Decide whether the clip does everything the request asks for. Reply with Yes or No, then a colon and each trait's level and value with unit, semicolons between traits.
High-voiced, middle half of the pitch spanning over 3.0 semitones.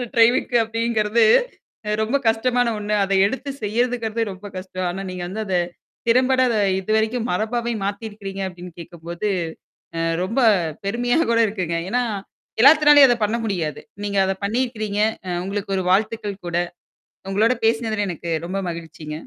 Yes: high, 215 Hz; average, 3.7 semitones